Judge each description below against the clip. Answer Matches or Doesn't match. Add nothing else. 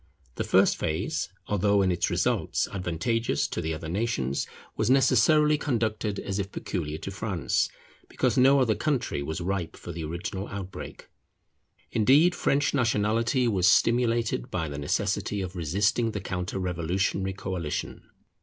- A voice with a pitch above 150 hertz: Doesn't match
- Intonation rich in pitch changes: Doesn't match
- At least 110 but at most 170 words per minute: Matches